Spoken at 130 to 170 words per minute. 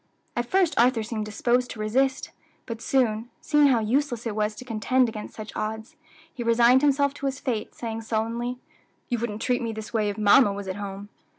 No: average, 200 wpm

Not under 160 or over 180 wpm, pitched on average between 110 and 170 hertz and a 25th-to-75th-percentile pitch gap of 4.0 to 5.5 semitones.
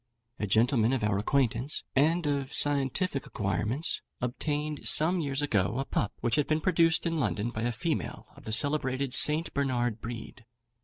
Yes: average, 165 wpm; low, 135 Hz; average, 4.7 semitones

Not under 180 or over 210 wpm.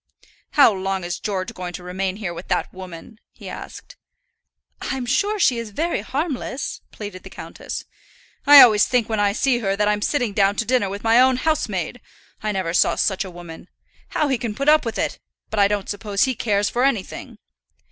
Yes: average, 200 wpm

